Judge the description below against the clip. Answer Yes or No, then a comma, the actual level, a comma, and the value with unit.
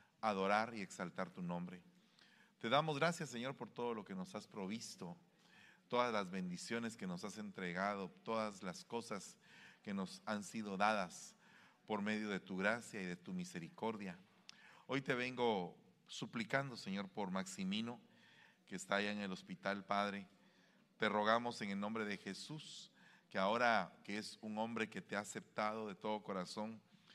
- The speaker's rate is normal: Yes, average, 165 wpm